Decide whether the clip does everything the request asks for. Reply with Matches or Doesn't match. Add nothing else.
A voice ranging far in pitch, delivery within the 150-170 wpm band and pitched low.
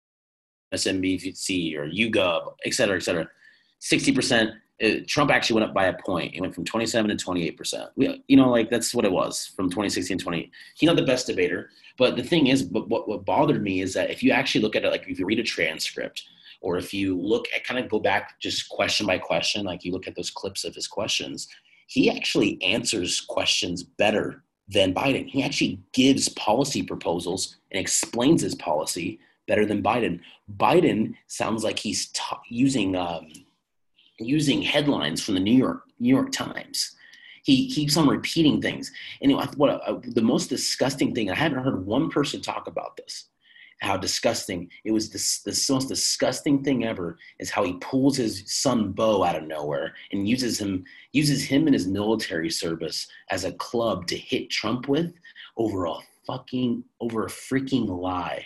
Doesn't match